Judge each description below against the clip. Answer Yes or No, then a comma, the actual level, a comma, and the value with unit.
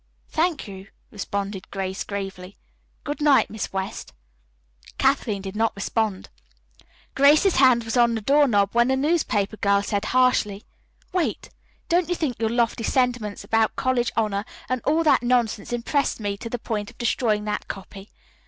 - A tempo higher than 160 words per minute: No, average, 155 wpm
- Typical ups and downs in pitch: Yes, average, 4.4 semitones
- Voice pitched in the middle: No, high, 225 Hz